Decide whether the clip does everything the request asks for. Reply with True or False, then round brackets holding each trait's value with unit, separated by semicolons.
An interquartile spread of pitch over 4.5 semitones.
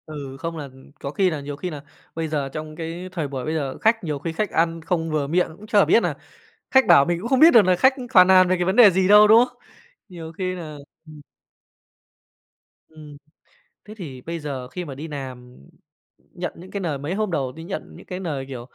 False (4.2 semitones)